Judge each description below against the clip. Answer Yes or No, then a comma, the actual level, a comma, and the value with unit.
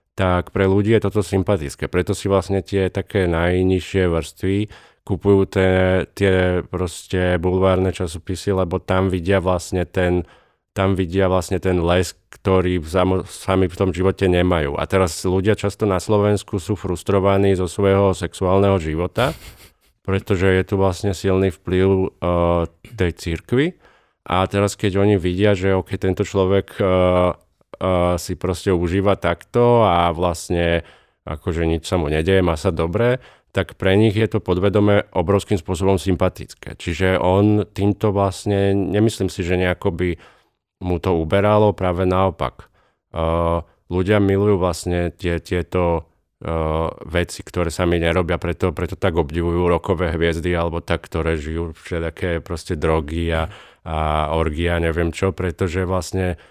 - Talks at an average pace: Yes, average, 145 wpm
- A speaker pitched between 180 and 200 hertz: No, very low, 95 Hz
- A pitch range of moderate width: No, narrow, 2.2 semitones